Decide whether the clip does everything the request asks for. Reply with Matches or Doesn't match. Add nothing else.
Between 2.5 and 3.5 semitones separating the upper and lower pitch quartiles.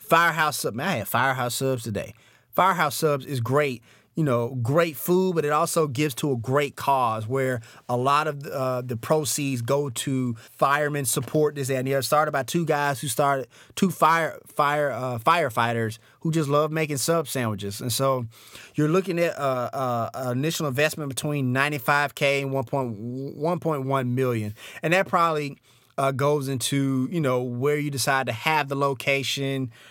Matches